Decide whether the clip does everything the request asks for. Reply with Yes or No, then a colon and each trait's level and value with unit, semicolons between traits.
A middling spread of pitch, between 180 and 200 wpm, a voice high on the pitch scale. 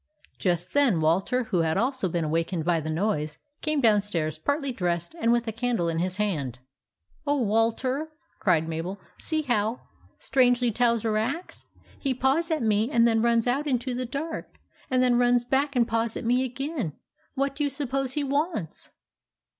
No: wide, 6.2 semitones; average, 185 wpm; high, 235 Hz